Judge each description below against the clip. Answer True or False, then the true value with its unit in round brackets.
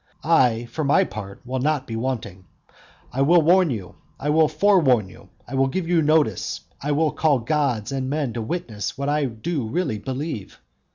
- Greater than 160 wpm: True (185 wpm)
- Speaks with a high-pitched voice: False (140 Hz)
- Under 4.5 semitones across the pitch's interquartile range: False (5.0 semitones)